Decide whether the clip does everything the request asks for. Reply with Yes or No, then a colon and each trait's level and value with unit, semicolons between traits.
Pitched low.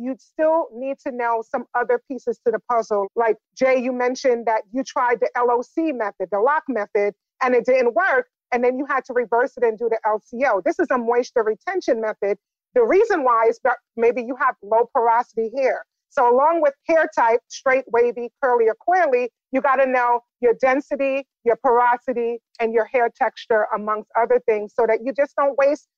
No: high, 245 Hz